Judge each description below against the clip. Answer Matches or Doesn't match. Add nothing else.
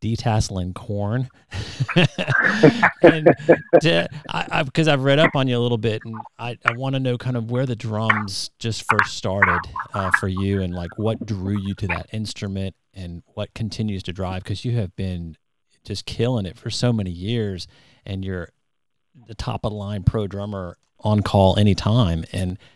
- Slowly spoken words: Doesn't match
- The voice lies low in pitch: Matches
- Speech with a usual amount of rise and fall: Matches